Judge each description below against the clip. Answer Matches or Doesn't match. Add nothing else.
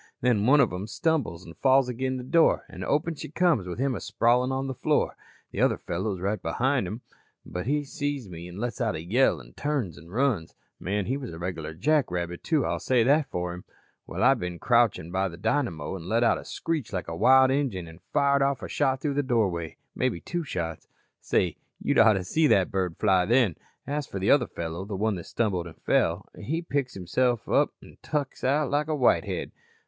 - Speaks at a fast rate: Matches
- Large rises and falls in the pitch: Matches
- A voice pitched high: Doesn't match